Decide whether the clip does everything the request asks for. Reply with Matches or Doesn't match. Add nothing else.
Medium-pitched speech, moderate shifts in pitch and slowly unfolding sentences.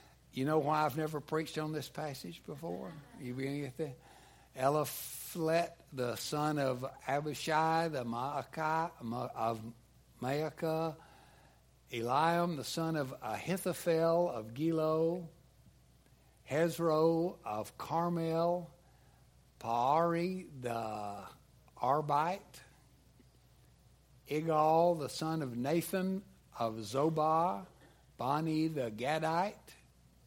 Matches